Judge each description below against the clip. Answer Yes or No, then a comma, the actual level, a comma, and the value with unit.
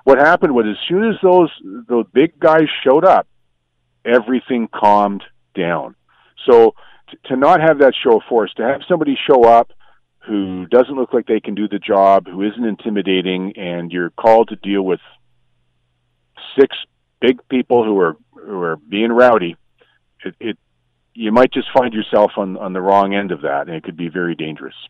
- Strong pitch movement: Yes, wide, 6.3 semitones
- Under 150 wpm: No, average, 185 wpm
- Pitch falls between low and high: No, low, 100 Hz